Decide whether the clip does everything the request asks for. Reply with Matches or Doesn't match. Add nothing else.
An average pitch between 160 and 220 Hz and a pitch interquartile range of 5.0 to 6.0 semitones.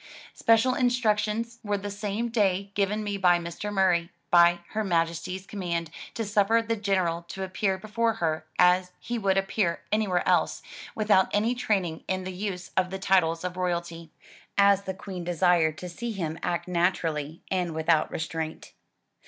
Doesn't match